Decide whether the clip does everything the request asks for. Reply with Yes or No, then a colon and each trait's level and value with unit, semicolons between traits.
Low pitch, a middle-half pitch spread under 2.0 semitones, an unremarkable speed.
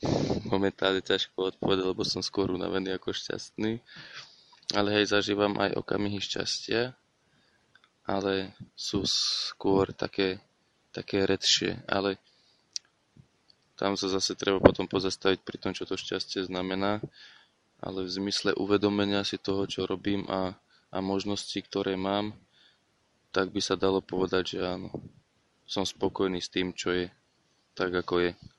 Yes: very low, 95 Hz; narrow, 1.1 semitones; average, 130 wpm